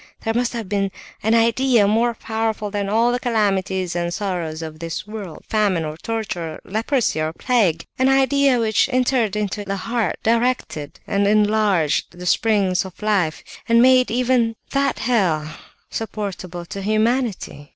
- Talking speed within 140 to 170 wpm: Yes, average, 150 wpm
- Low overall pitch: No, high, 215 Hz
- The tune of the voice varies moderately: Yes, average, 4.0 semitones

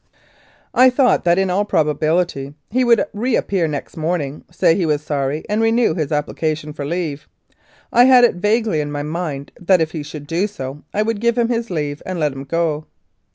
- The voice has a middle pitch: Yes, medium, 165 Hz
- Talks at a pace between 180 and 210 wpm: Yes, average, 200 wpm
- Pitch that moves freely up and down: Yes, wide, 5.9 semitones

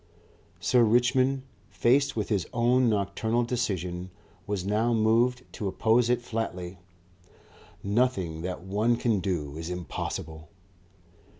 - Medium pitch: No, low, 110 Hz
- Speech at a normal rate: No, slow, 115 wpm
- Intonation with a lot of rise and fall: No, average, 4.7 semitones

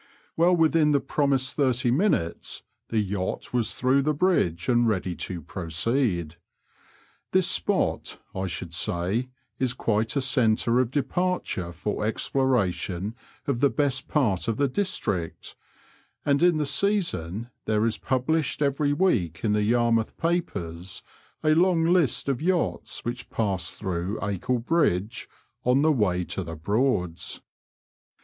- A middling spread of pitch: No, wide, 7.1 semitones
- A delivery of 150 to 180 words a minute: No, average, 140 wpm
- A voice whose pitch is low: Yes, low, 120 Hz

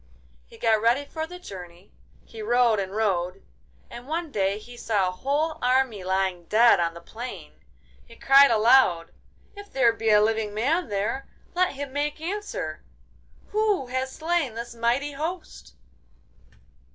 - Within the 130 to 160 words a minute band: Yes, average, 150 wpm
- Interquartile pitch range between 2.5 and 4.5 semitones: No, wide, 5.6 semitones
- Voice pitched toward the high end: Yes, high, 235 Hz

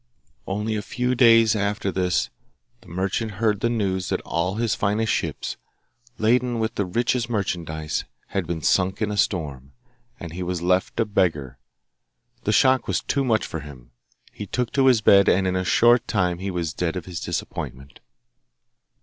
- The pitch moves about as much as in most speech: Yes, average, 4.3 semitones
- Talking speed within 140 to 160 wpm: No, average, 175 wpm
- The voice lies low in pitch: Yes, low, 100 Hz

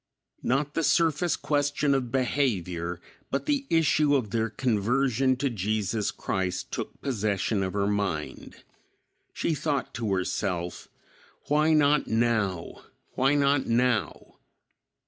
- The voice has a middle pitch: No, low, 125 Hz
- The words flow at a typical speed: No, slow, 120 wpm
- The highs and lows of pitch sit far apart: Yes, wide, 6.0 semitones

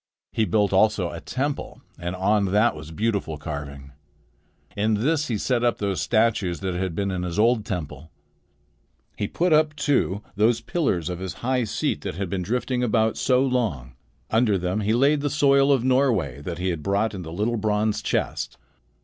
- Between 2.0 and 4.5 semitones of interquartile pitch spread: No, average, 5.3 semitones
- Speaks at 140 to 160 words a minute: No, average, 185 wpm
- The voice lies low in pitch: Yes, low, 105 Hz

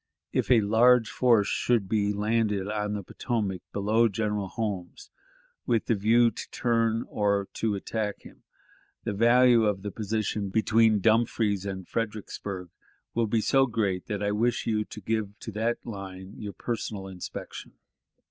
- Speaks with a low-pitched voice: Yes, low, 105 Hz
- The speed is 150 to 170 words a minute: Yes, average, 155 wpm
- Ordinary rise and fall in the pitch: No, narrow, 2.1 semitones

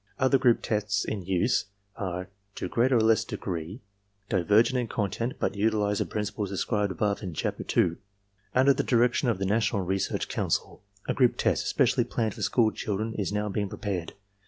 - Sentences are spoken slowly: No, average, 180 wpm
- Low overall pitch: Yes, low, 105 Hz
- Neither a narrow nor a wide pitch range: Yes, average, 3.1 semitones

